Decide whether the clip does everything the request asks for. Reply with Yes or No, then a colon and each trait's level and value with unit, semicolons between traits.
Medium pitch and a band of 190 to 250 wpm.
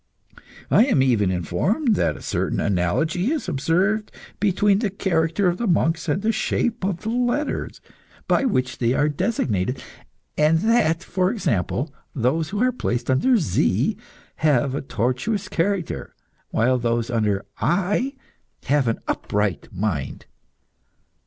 No: medium, 160 Hz; average, 140 wpm